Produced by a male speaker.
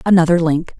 No: female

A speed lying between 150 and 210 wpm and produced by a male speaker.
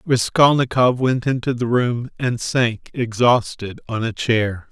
No: average, 140 wpm; male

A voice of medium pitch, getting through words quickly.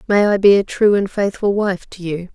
No: high, 195 Hz; fast, 255 wpm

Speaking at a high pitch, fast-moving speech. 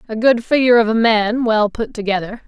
Yes: high, 225 Hz; fast, 220 wpm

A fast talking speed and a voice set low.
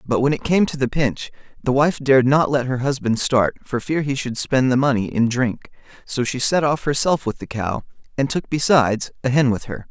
Yes: fast, 235 wpm; low, 130 Hz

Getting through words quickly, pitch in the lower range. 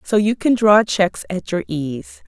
No: fast, 210 wpm; high, 195 Hz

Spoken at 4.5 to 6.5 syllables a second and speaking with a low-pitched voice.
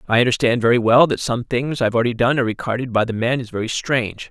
No: 7.0 syllables/s; low, 120 Hz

